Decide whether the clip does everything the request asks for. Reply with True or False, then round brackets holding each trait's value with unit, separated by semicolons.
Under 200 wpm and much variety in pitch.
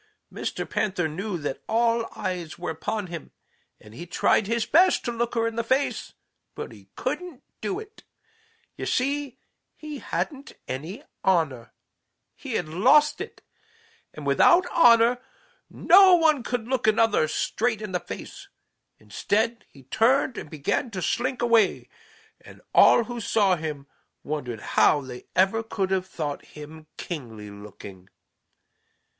True (145 wpm; 7.8 semitones)